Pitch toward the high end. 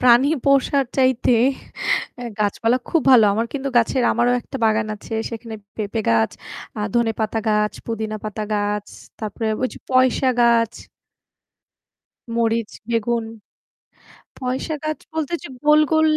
Yes: high, 235 Hz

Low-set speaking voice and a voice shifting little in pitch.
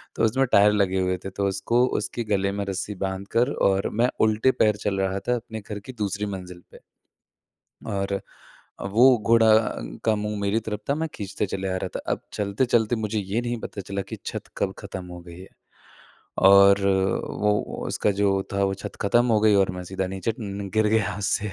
Yes: low, 100 Hz; narrow, 2.2 semitones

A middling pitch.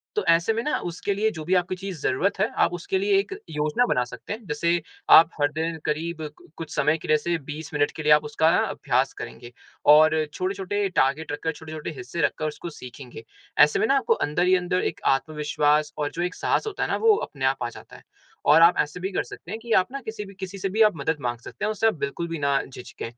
Yes: medium, 165 Hz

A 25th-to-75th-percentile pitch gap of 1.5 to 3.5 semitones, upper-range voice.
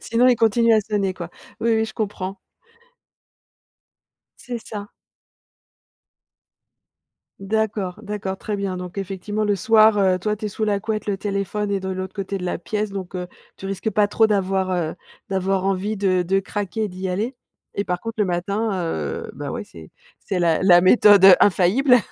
Yes: narrow, 2.4 semitones; high, 200 Hz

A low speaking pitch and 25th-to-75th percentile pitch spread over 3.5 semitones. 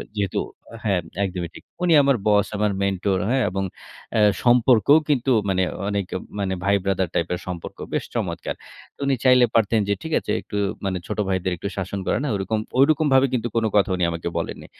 Yes: low, 100 Hz; average, 4.6 semitones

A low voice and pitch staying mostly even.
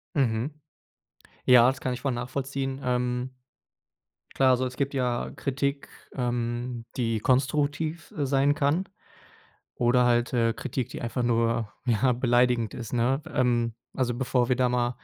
Yes: low, 125 Hz; narrow, 2.0 semitones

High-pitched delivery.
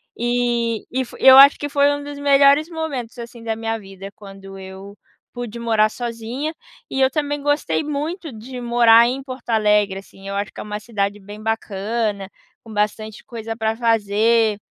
Yes: high, 230 Hz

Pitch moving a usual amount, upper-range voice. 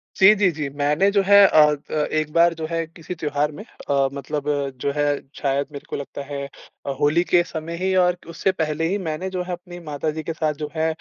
No: average, 3.0 semitones; medium, 160 Hz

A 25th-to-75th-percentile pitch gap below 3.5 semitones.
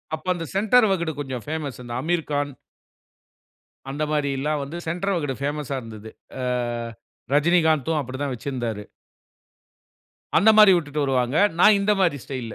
No: average, 4.2 semitones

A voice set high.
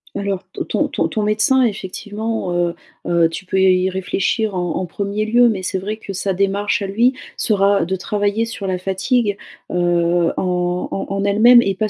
Yes: high, 195 Hz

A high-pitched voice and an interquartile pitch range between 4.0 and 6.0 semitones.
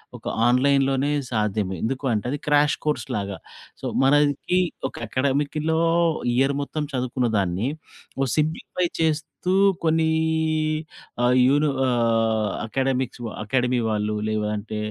No: low, 130 Hz; average, 4.9 semitones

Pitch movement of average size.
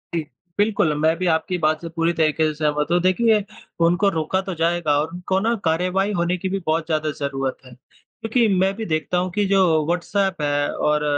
Yes: average, 3.5 semitones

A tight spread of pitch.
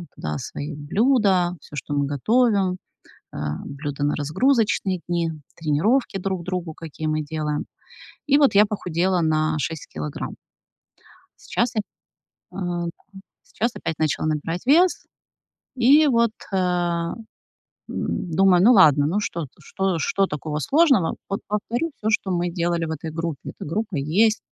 No: average, 5.3 semitones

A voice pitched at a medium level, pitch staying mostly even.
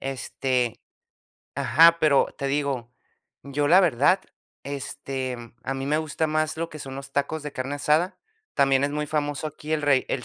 Yes: medium, 145 Hz; narrow, 2.3 semitones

